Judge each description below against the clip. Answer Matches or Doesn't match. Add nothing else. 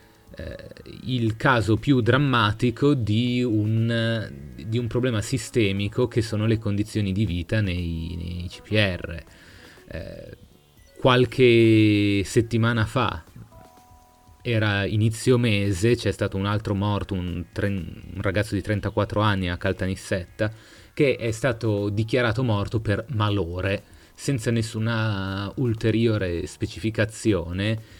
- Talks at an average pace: Doesn't match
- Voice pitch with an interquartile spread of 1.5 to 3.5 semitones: Matches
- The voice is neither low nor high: Doesn't match